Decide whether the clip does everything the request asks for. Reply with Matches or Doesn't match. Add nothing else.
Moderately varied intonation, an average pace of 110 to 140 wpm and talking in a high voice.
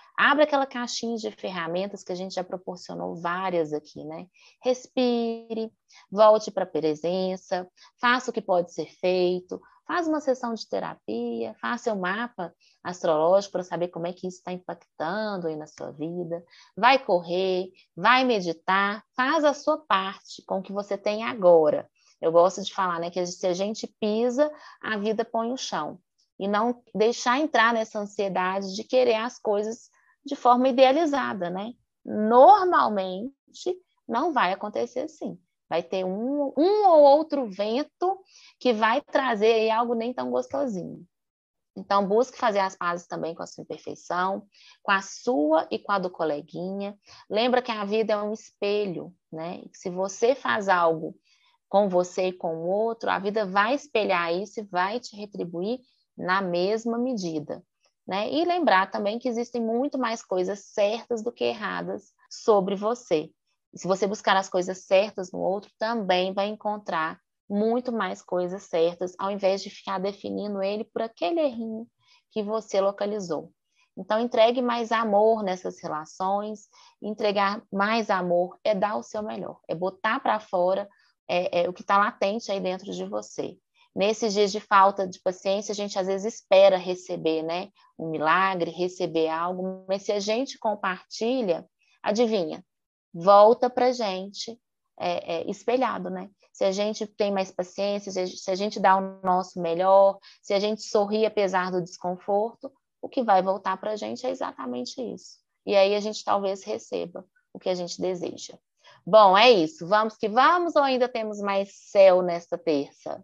Doesn't match